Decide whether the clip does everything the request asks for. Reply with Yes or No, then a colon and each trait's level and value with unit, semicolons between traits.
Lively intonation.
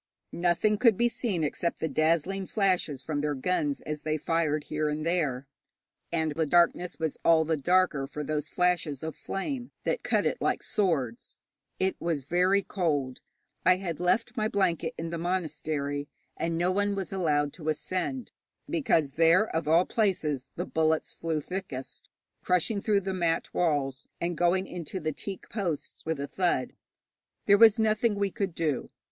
No: average, 3.9 semitones